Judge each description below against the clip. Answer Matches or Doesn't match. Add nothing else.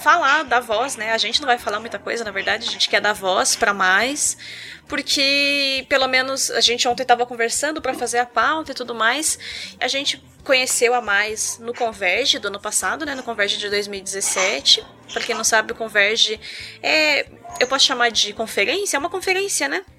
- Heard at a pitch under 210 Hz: Doesn't match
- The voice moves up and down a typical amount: Matches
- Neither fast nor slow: Doesn't match